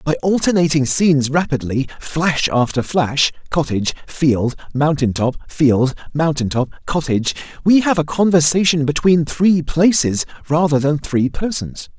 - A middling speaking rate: No, slow, 130 wpm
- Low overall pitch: No, medium, 150 Hz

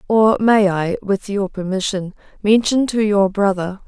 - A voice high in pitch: Yes, high, 200 Hz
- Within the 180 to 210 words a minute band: No, average, 155 wpm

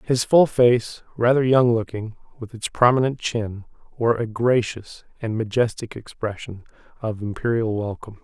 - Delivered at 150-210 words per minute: No, average, 140 wpm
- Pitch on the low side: Yes, low, 115 Hz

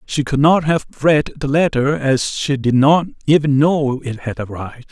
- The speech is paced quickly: No, average, 195 wpm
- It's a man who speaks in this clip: Yes, male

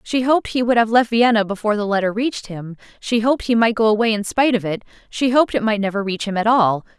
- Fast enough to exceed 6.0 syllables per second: Yes, 6.7 syllables/s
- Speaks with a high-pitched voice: Yes, high, 220 Hz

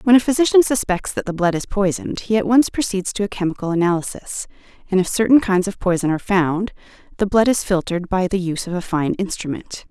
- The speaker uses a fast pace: Yes, fast, 220 wpm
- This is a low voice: No, high, 195 Hz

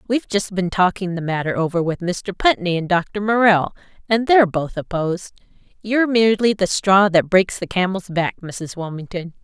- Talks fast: No, average, 180 wpm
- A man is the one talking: No, female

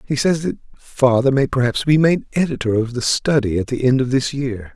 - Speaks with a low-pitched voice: Yes, low, 130 Hz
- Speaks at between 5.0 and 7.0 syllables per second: Yes, 5.2 syllables/s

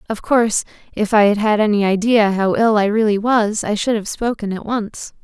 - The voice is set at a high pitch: Yes, high, 215 Hz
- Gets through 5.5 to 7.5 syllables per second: No, 5.1 syllables/s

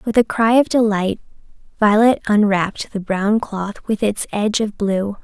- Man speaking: No, female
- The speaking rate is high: No, average, 170 wpm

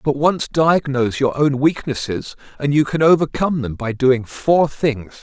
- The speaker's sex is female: No, male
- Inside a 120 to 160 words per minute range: No, average, 170 wpm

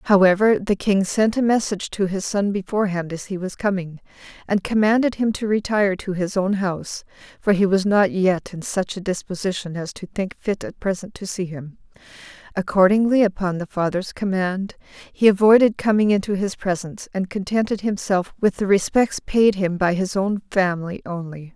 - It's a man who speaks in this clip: No, female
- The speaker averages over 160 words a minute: Yes, average, 180 wpm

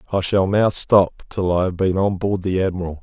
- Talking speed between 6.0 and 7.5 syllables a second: No, 5.1 syllables/s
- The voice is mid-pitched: No, very low, 95 Hz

